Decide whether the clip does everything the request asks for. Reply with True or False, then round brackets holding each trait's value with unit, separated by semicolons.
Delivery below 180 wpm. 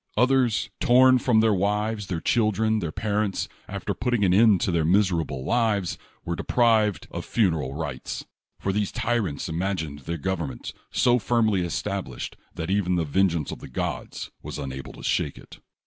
True (165 wpm)